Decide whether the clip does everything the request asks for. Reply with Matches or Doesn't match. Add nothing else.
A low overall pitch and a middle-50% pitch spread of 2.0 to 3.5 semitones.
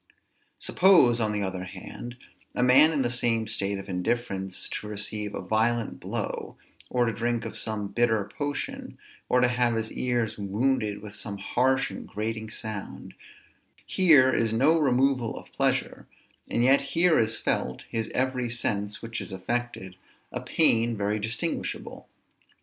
Matches